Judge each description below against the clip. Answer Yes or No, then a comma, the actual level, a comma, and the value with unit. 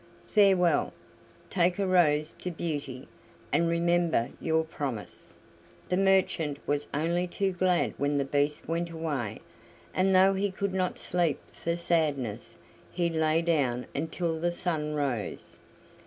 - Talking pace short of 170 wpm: Yes, slow, 135 wpm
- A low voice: No, medium, 165 Hz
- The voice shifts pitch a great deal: No, average, 3.5 semitones